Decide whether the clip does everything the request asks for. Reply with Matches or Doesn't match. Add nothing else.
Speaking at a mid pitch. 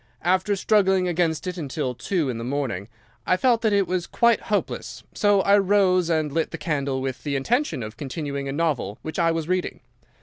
Matches